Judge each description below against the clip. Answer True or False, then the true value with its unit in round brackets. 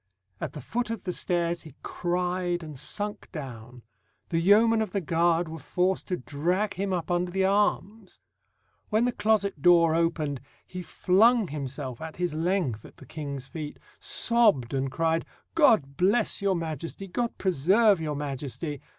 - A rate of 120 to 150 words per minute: False (160 wpm)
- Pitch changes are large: False (4.8 semitones)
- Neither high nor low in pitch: True (175 Hz)